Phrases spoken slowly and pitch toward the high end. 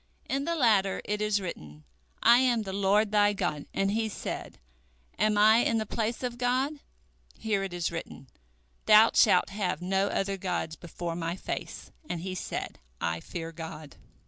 No: average, 170 wpm; high, 200 Hz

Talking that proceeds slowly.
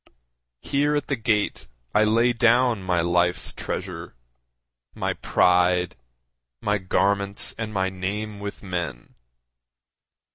Yes: slow, 110 wpm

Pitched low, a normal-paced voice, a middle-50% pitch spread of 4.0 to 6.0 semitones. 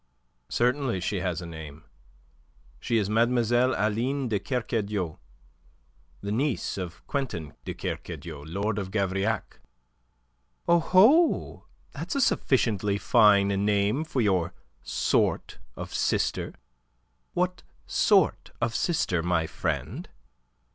No: low, 105 Hz; slow, 105 wpm; average, 5.1 semitones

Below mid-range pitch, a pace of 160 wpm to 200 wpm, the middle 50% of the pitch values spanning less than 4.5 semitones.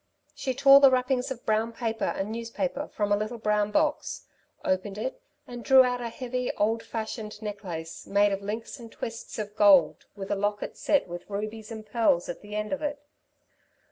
No: high, 220 Hz; average, 190 wpm; average, 3.3 semitones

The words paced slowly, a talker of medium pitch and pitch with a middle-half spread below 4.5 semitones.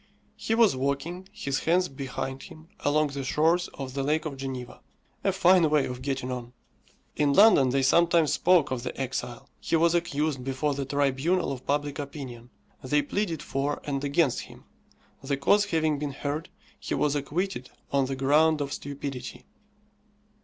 No: average, 165 wpm; medium, 145 Hz; average, 3.1 semitones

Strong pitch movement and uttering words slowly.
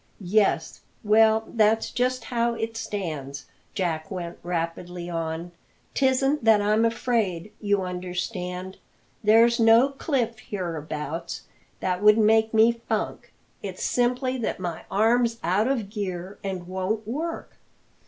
No: average, 4.3 semitones; slow, 125 wpm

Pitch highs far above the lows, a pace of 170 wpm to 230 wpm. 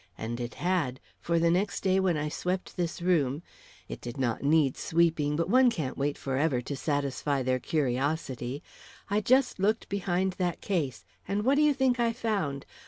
Yes: wide, 5.7 semitones; average, 180 wpm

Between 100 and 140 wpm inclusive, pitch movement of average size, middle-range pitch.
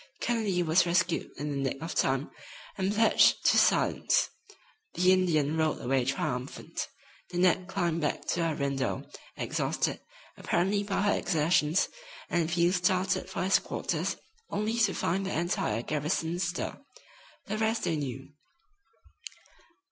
Yes: slow, 135 wpm; average, 4.1 semitones; medium, 170 Hz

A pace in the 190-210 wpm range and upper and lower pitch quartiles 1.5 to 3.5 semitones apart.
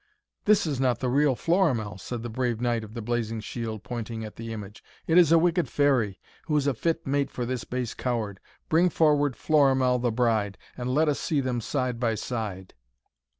No: average, 200 wpm; average, 4.2 semitones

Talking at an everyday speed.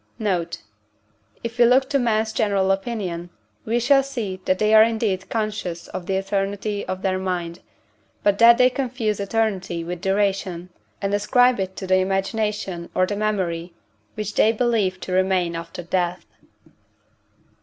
Yes: average, 155 wpm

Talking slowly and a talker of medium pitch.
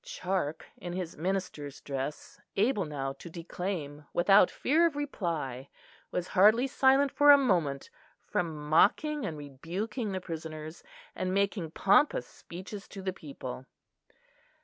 Yes: slow, 130 wpm; medium, 180 Hz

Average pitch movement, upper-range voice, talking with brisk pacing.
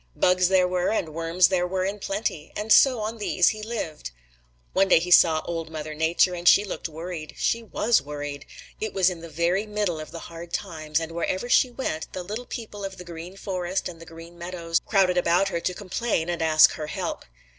No: average, 3.0 semitones; medium, 180 Hz; fast, 210 wpm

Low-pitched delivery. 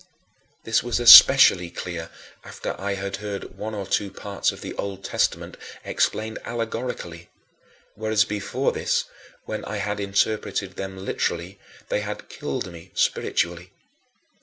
Yes: low, 100 Hz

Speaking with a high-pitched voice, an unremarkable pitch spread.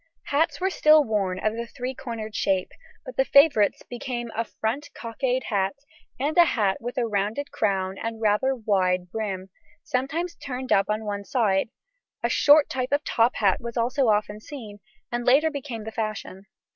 Yes: high, 230 Hz; average, 4.2 semitones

